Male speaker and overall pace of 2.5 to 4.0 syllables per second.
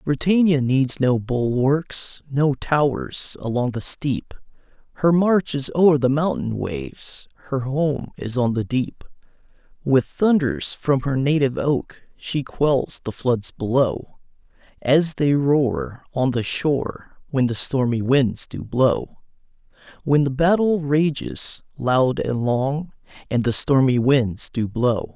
Yes: male; 3.6 syllables/s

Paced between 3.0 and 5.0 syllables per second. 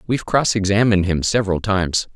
No: 6.6 syllables/s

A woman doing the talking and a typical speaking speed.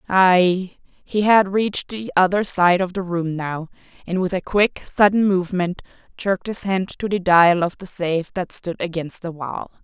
Yes: female; average, 185 wpm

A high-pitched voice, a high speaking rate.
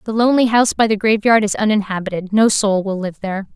Yes: high, 210 Hz; fast, 220 wpm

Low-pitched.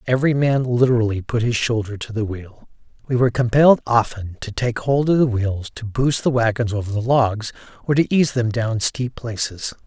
Yes: low, 120 Hz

